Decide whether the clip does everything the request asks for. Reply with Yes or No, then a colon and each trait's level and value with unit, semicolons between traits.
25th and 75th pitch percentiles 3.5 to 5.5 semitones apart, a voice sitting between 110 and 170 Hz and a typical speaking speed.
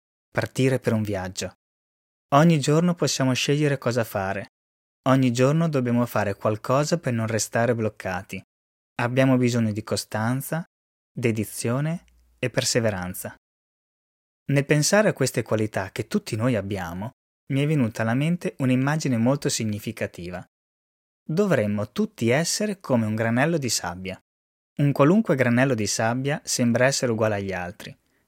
Yes: average, 5.1 semitones; low, 120 Hz; average, 130 wpm